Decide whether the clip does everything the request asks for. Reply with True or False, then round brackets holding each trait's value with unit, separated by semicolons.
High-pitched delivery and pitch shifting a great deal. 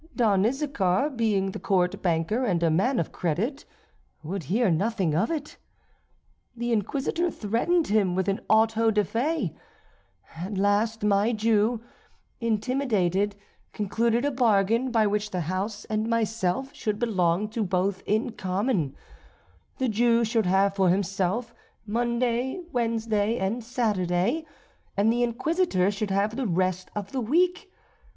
False (215 Hz; 3.8 semitones)